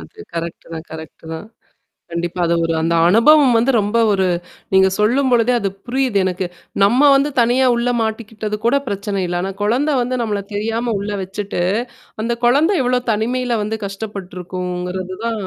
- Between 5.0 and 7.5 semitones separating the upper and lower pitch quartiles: No, average, 4.5 semitones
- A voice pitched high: Yes, high, 210 Hz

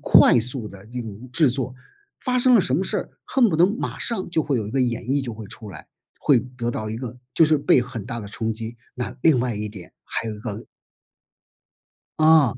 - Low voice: Yes, low, 125 Hz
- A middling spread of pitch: Yes, average, 4.6 semitones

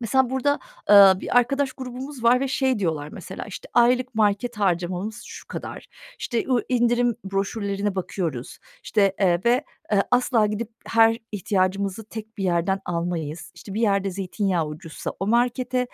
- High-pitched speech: Yes, high, 210 Hz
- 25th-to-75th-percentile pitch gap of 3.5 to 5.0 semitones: Yes, average, 4.3 semitones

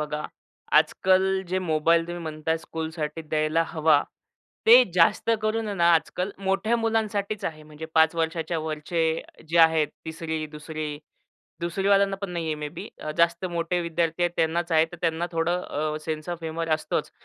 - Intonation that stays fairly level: Yes, narrow, 2.1 semitones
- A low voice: No, medium, 165 Hz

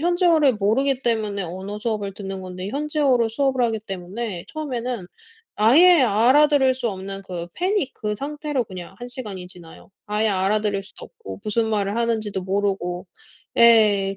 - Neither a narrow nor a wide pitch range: Yes, average, 4.9 semitones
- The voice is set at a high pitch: Yes, high, 215 Hz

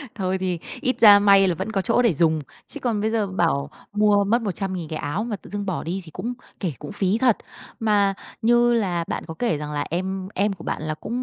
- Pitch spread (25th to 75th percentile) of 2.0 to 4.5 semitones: Yes, average, 3.9 semitones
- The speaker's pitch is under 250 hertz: Yes, high, 195 Hz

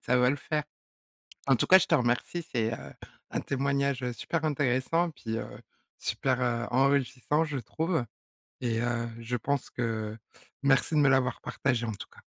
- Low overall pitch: Yes, low, 130 Hz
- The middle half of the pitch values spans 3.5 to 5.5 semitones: No, average, 2.9 semitones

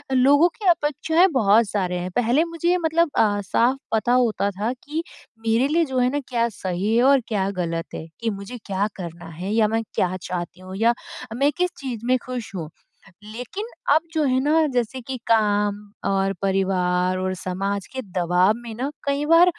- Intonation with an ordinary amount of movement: No, wide, 6.0 semitones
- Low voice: No, high, 225 Hz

